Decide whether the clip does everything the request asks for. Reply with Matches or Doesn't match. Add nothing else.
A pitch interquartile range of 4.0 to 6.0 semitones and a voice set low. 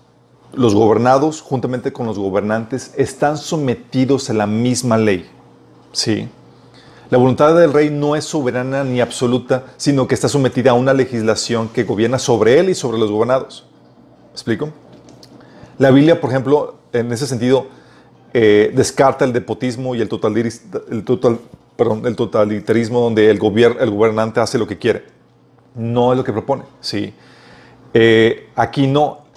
Doesn't match